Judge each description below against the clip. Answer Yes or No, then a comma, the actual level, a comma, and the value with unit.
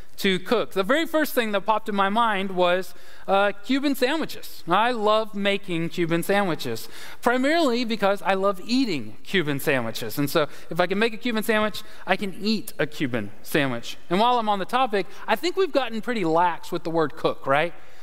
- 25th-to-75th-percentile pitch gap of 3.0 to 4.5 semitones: No, average, 5.1 semitones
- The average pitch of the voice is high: Yes, high, 200 Hz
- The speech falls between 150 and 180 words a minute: No, average, 195 wpm